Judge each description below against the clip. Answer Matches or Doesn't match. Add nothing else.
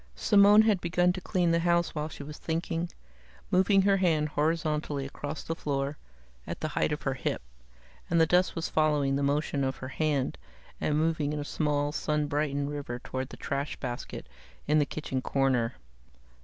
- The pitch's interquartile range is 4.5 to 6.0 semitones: Doesn't match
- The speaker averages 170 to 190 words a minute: Matches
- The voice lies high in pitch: Doesn't match